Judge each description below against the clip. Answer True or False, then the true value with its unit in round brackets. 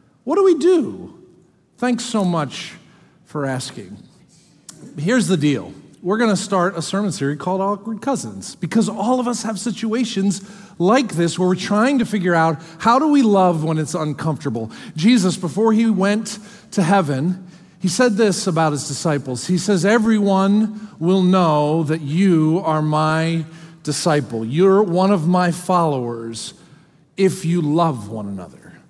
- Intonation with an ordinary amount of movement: True (4.5 semitones)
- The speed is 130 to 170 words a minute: True (155 wpm)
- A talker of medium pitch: True (180 Hz)